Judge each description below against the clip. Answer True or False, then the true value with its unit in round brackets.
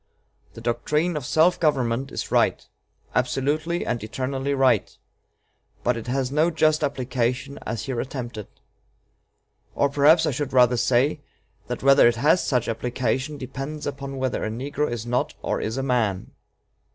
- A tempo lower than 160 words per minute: True (150 wpm)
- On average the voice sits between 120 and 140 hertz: True (135 Hz)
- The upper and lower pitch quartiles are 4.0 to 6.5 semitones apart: False (3.0 semitones)